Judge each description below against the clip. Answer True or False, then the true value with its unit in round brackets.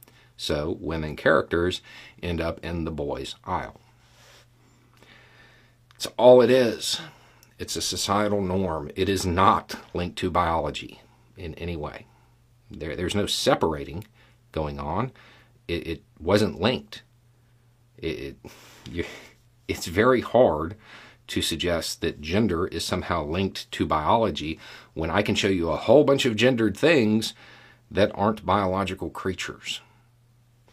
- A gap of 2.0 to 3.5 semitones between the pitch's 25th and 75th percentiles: False (5.2 semitones)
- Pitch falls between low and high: False (105 Hz)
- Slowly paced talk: True (120 wpm)